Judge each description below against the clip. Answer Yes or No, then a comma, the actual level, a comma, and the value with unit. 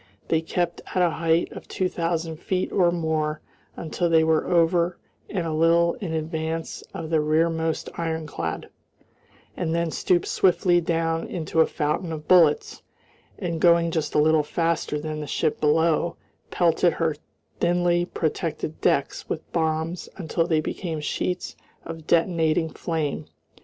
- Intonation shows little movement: Yes, narrow, 1.4 semitones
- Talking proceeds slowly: No, average, 145 wpm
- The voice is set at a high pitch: No, medium, 165 Hz